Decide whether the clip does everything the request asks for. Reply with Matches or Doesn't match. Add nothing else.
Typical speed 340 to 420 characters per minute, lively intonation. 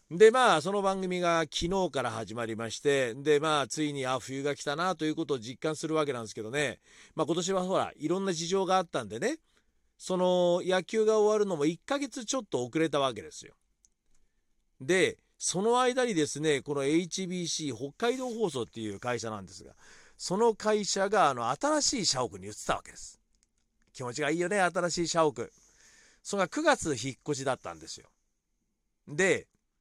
Matches